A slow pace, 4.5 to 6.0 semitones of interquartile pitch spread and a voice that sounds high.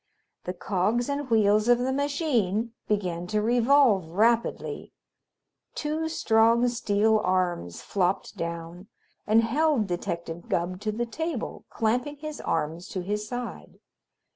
Yes: slow, 125 wpm; average, 5.1 semitones; high, 220 Hz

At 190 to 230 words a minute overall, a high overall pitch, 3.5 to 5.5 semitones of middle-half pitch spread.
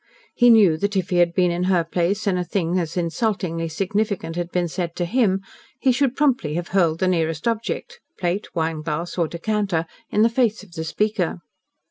No: average, 195 wpm; medium, 180 Hz; average, 3.9 semitones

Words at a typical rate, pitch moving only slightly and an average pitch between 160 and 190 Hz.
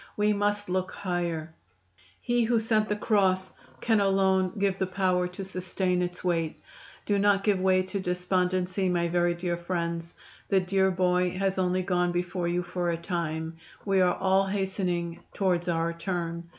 Yes: average, 165 wpm; narrow, 1.8 semitones; medium, 185 Hz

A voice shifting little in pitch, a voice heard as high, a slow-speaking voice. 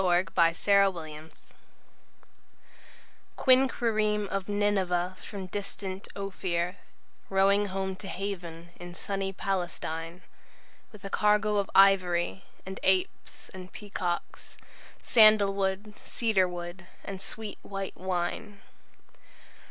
Yes: narrow, 2.2 semitones; high, 195 Hz; slow, 85 wpm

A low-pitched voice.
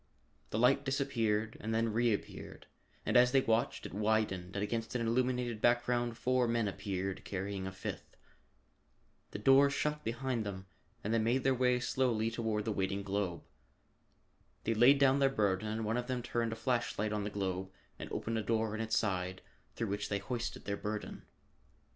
Yes: low, 115 Hz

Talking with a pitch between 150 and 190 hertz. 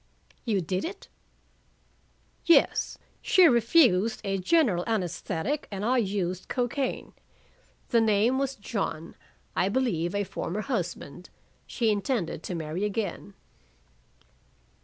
No: high, 205 Hz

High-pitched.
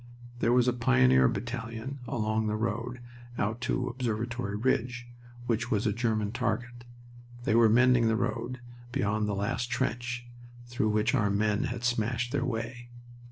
No: low, 115 Hz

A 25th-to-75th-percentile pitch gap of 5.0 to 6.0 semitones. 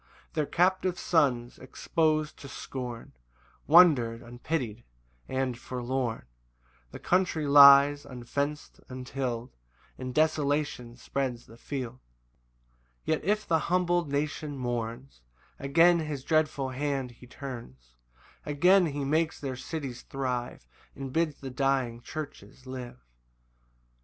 No: average, 3.7 semitones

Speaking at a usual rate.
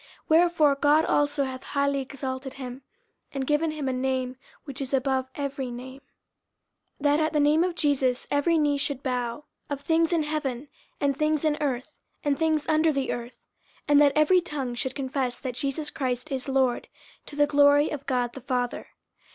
Yes: average, 190 wpm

